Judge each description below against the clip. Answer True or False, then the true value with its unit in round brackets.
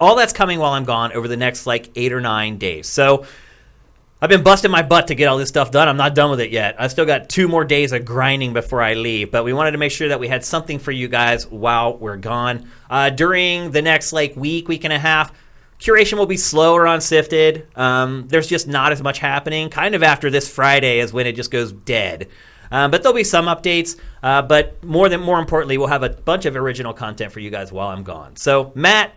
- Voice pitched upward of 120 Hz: True (140 Hz)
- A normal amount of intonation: True (4.7 semitones)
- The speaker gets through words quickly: True (245 wpm)